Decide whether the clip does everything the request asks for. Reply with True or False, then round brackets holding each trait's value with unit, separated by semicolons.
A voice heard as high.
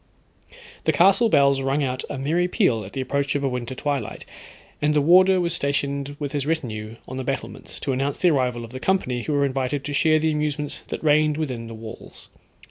False (140 Hz)